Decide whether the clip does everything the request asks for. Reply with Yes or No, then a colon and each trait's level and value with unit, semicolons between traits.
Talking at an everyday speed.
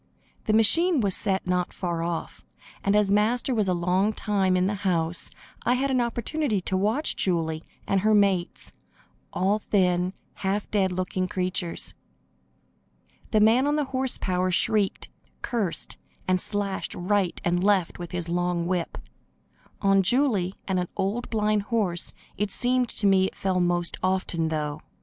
Yes: average, 160 wpm